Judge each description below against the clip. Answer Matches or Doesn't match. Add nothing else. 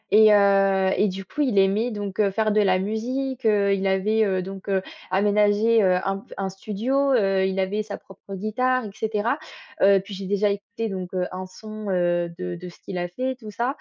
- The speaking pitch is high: Matches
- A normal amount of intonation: Doesn't match